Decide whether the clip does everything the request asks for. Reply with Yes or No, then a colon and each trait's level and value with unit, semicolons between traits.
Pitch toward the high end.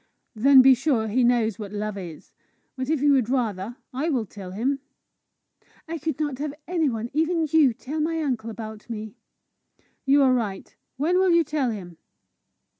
Yes: very high, 255 Hz